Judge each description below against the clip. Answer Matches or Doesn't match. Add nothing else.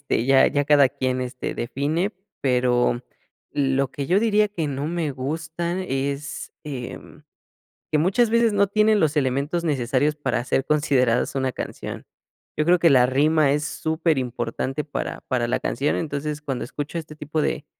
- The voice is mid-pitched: Matches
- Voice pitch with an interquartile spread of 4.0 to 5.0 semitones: Doesn't match